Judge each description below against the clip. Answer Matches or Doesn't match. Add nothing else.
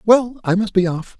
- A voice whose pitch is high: Matches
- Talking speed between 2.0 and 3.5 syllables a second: Doesn't match